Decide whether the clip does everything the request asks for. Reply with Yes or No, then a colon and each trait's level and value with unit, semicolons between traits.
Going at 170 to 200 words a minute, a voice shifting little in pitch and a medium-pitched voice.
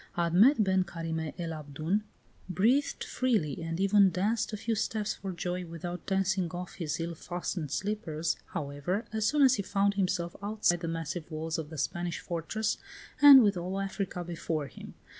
No: average, 175 wpm; average, 3.6 semitones; medium, 180 Hz